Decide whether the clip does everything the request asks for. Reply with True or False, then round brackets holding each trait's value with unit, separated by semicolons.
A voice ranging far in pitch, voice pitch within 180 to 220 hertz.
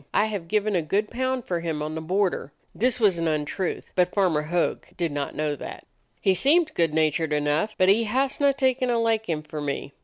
True (6.4 semitones; 185 Hz)